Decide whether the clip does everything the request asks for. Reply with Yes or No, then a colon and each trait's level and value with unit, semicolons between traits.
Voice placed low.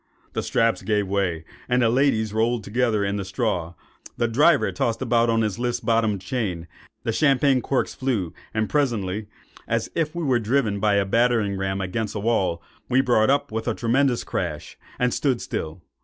Yes: low, 115 Hz